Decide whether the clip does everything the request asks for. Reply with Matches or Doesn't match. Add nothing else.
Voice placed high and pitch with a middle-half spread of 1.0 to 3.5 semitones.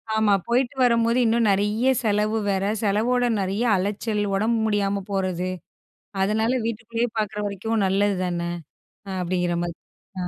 Matches